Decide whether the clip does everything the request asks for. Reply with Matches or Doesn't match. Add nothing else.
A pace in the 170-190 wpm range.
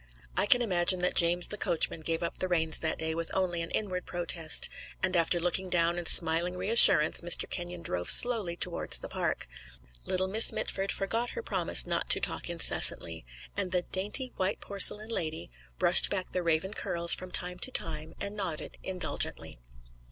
Matches